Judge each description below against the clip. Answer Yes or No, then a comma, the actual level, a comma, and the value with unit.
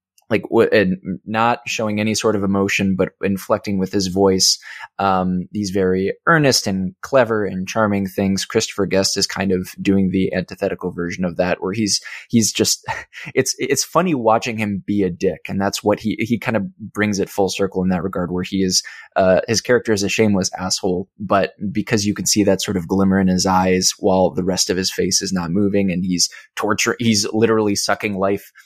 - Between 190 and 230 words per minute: Yes, fast, 205 wpm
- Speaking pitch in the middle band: No, low, 100 Hz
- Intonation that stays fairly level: Yes, narrow, 2.3 semitones